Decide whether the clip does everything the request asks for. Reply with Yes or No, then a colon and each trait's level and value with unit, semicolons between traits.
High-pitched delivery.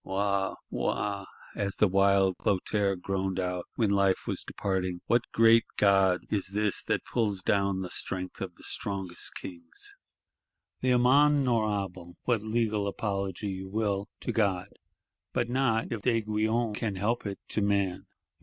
No: low, 100 Hz